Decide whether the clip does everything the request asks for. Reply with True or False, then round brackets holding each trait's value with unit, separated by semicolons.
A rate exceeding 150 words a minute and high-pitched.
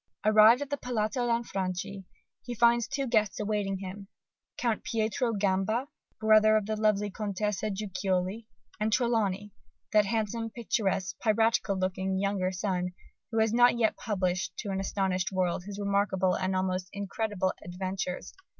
False (140 wpm; 205 Hz)